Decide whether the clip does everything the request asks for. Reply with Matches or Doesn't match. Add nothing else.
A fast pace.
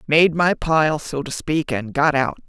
Matches